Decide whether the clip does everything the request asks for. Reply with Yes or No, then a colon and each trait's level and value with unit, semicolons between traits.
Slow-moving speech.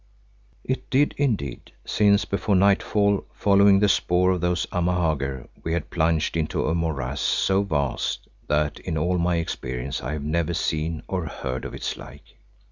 No: average, 160 wpm